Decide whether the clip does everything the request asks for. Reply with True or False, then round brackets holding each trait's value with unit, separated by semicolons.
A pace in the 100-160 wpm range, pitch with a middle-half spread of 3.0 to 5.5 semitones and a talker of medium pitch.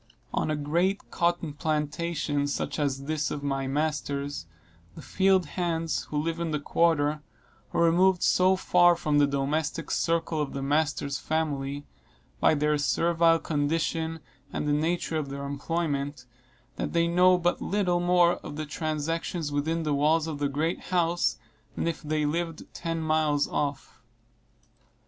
False (155 wpm; 2.6 semitones; 155 Hz)